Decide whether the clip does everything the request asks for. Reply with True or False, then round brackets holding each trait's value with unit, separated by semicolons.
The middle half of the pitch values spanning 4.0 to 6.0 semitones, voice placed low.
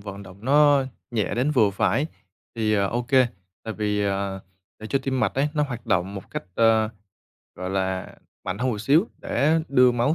True (5.0 semitones; 115 Hz)